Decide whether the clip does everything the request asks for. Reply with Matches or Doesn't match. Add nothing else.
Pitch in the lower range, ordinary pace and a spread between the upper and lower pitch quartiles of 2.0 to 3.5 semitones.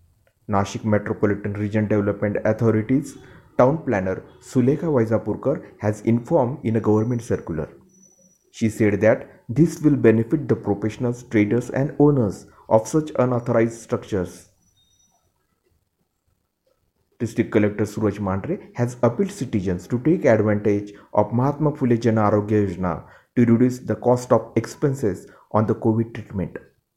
Matches